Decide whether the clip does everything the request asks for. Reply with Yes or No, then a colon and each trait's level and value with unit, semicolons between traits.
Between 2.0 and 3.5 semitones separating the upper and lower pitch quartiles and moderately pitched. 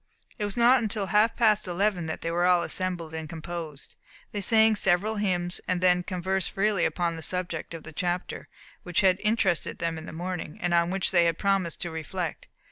Yes: average, 2.8 semitones; medium, 180 Hz